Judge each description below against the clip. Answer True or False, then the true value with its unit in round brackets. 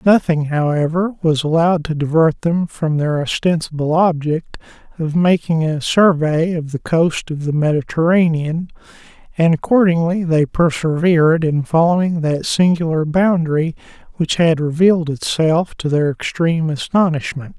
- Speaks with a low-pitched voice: False (160 Hz)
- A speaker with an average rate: False (130 wpm)